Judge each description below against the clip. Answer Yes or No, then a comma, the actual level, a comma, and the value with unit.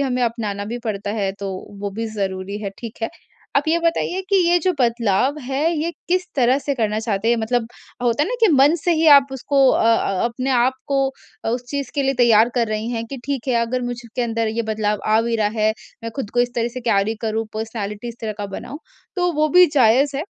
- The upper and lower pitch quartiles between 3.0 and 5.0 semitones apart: Yes, average, 3.9 semitones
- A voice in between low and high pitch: No, high, 235 Hz